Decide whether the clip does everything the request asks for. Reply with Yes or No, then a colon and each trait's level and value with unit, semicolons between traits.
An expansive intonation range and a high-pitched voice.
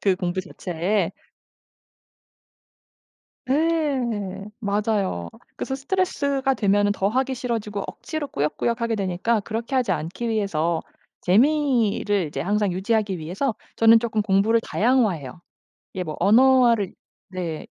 No: average, 4.8 semitones; high, 210 Hz